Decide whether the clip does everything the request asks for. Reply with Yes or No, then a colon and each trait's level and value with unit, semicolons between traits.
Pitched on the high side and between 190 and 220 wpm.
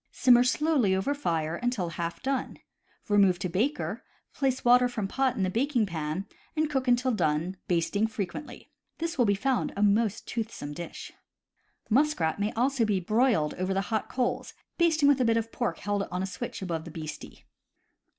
No: high, 220 Hz; average, 180 wpm